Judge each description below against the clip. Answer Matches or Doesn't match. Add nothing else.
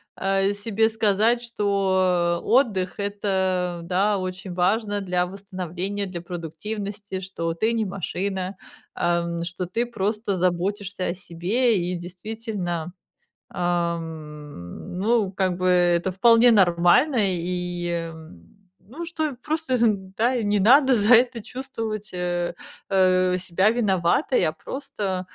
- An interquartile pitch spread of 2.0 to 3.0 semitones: Doesn't match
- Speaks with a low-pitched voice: Doesn't match